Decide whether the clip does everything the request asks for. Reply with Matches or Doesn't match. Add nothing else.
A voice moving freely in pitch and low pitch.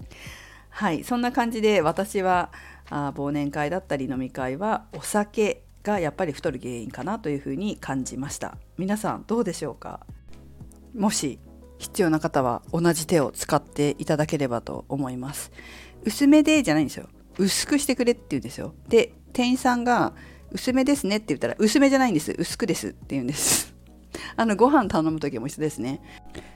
Doesn't match